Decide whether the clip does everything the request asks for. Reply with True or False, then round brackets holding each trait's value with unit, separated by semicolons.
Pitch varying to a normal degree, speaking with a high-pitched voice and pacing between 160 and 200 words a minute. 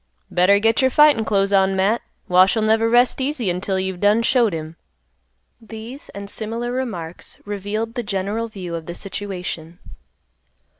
False (3.3 semitones; 205 Hz; 150 wpm)